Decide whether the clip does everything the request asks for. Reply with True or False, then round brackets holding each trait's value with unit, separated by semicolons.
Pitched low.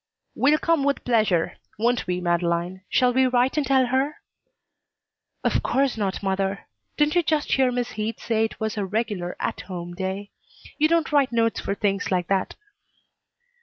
False (225 Hz)